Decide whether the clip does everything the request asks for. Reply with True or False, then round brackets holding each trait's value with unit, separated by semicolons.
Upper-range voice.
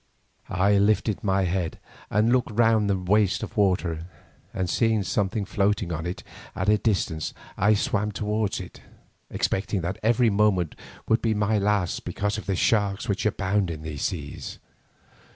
False (100 Hz)